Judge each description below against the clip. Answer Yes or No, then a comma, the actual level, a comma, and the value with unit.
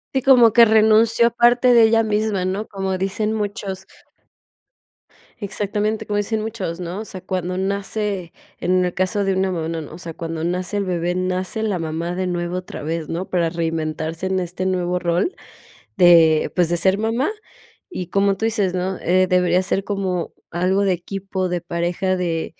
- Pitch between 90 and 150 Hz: No, medium, 185 Hz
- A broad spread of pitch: No, average, 2.9 semitones